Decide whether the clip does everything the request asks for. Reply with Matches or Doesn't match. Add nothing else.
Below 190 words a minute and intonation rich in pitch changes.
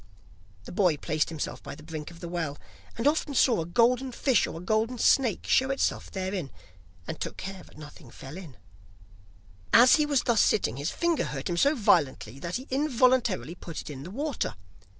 Doesn't match